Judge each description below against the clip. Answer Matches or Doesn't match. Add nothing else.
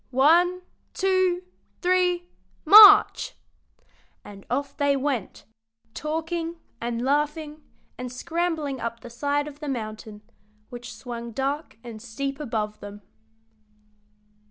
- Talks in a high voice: Matches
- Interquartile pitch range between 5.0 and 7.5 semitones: Matches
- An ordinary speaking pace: Doesn't match